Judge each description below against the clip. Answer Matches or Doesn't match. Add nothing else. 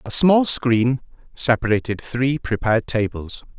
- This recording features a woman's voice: Doesn't match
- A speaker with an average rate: Doesn't match